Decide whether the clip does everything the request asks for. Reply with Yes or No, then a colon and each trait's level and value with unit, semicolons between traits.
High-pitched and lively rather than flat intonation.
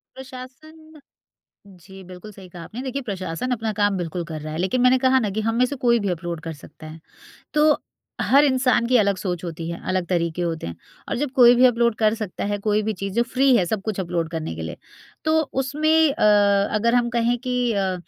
Yes: high, 210 Hz; wide, 6.1 semitones